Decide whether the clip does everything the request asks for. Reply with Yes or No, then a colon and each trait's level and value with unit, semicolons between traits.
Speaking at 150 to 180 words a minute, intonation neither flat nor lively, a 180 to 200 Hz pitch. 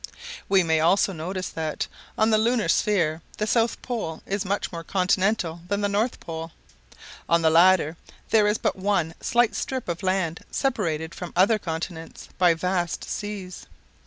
Yes: average, 160 wpm; average, 3.9 semitones; medium, 185 Hz